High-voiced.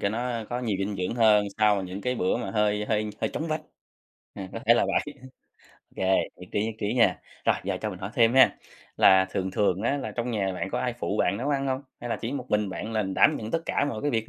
No: low, 110 Hz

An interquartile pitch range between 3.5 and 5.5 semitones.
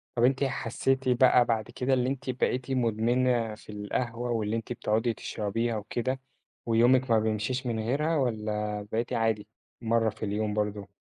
No: average, 2.8 semitones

